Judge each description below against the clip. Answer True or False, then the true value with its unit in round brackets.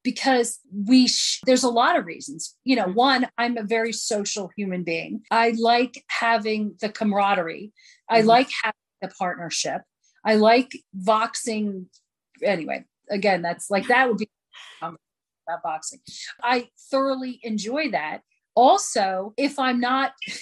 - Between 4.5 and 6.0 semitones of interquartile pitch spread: False (3.4 semitones)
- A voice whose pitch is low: False (230 Hz)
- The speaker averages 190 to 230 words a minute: False (140 wpm)